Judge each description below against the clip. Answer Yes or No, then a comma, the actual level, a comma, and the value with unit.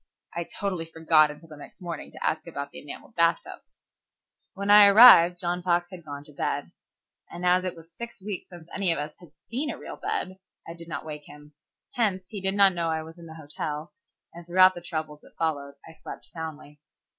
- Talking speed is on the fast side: Yes, fast, 215 wpm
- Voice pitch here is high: No, medium, 170 Hz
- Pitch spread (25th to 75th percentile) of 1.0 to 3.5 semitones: Yes, average, 2.9 semitones